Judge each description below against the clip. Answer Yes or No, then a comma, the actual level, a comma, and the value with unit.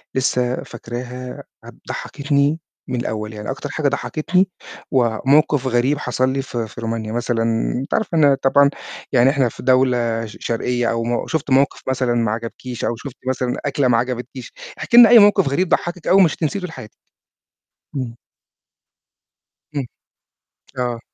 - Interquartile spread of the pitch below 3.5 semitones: Yes, average, 3.1 semitones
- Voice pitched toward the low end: Yes, low, 130 Hz